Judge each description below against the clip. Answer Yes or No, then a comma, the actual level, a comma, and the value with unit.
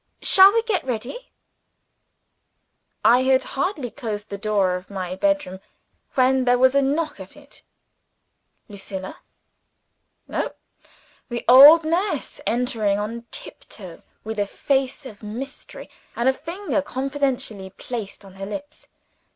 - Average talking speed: No, slow, 125 wpm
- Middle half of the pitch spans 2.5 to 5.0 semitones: No, wide, 5.5 semitones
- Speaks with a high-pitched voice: Yes, very high, 250 Hz